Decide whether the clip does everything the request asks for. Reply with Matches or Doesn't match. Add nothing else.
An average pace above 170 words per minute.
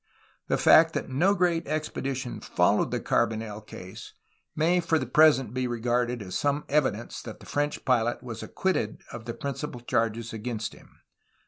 Matches